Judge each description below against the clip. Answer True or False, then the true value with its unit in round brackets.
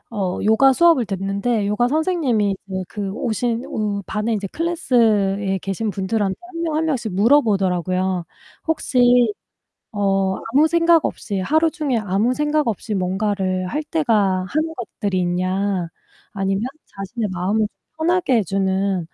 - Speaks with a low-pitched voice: False (210 Hz)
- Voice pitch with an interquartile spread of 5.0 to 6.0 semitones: True (5.3 semitones)